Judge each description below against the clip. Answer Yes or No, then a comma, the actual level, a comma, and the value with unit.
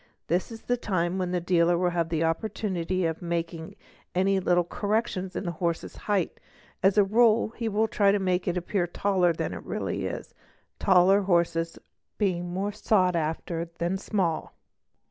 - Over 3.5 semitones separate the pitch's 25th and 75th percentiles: No, average, 2.8 semitones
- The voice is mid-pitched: Yes, medium, 180 Hz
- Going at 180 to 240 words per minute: Yes, average, 190 wpm